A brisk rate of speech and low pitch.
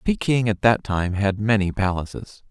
No: average, 170 wpm; low, 105 Hz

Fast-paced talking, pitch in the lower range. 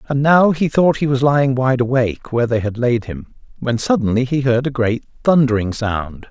Yes: fast, 210 wpm; low, 125 Hz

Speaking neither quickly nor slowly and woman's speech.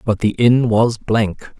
No: average, 190 wpm; male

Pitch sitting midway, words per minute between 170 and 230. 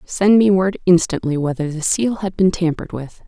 Yes: medium, 180 Hz; average, 200 wpm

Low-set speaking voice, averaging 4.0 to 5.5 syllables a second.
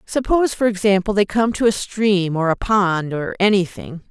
No: high, 200 Hz; 4.9 syllables/s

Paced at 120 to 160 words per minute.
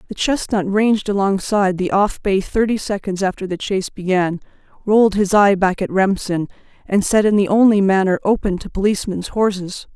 No: average, 175 wpm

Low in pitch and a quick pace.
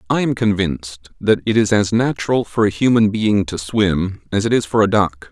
Yes: low, 105 Hz; fast, 225 wpm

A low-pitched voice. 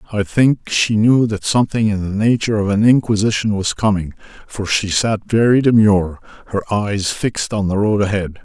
Yes: low, 105 Hz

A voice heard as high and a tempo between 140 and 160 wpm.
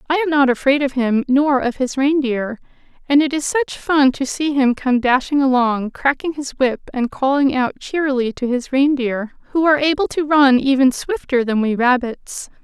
No: very high, 270 Hz; average, 195 wpm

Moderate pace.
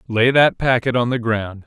No: fast, 215 wpm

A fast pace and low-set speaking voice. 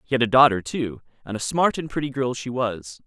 Yes: fast, 255 wpm; low, 120 Hz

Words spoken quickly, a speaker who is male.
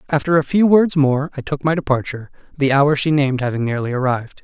Yes: fast, 215 wpm; male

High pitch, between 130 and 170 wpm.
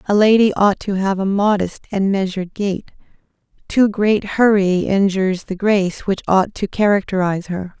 Yes: high, 195 Hz; average, 160 wpm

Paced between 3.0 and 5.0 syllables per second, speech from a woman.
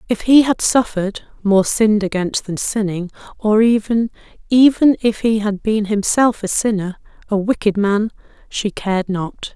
Yes: 4.6 syllables/s; female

